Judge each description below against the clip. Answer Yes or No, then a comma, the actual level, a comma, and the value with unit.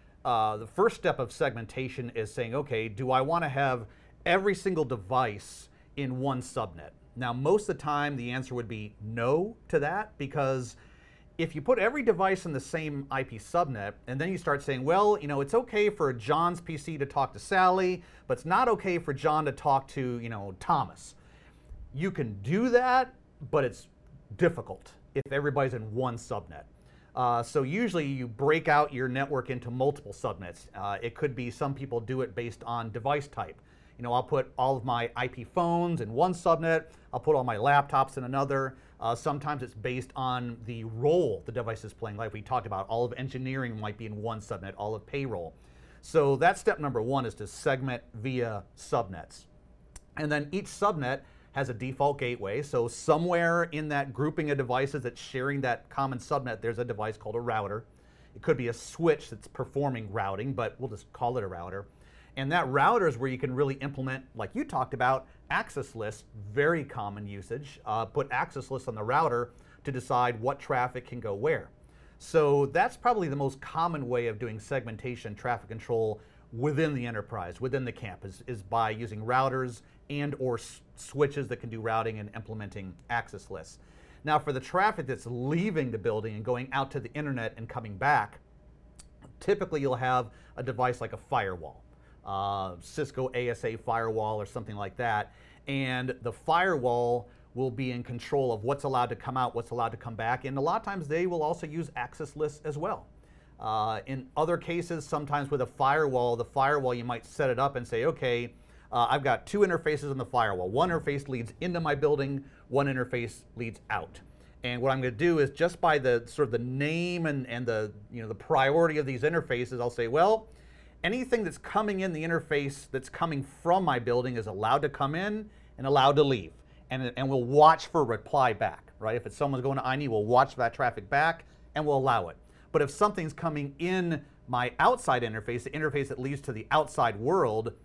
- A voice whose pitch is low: Yes, low, 130 Hz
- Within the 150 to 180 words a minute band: No, average, 195 wpm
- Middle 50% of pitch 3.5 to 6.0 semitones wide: Yes, average, 4.1 semitones